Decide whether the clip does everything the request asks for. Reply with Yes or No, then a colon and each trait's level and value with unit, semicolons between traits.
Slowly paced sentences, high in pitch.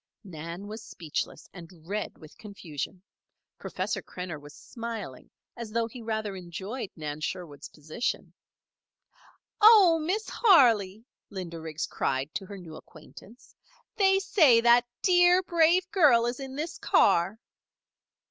Yes: slow, 130 wpm; high, 215 Hz